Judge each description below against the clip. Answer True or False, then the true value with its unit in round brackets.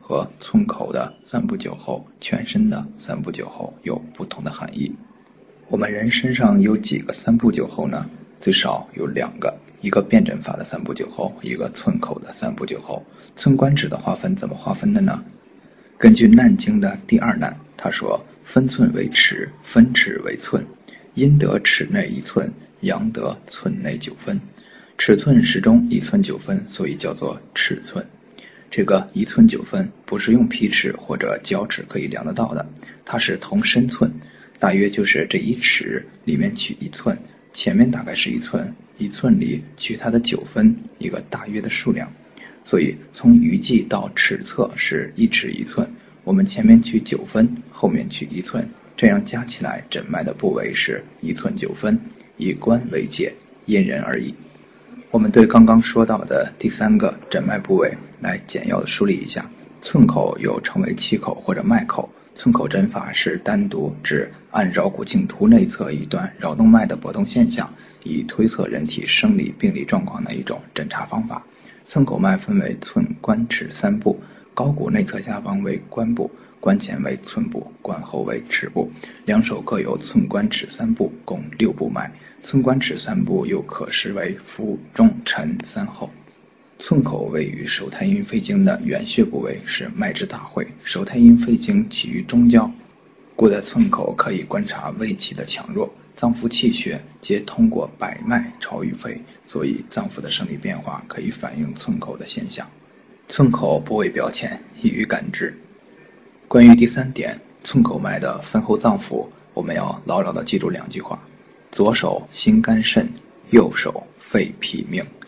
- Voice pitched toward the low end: False (210 Hz)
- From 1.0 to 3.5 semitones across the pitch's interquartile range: True (2.4 semitones)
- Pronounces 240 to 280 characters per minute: True (245 characters per minute)